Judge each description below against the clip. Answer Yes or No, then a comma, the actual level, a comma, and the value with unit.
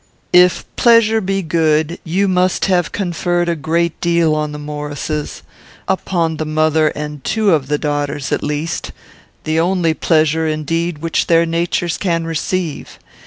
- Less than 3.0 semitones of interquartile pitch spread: Yes, narrow, 2.4 semitones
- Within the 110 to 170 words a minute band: Yes, average, 150 wpm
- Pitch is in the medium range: Yes, medium, 165 Hz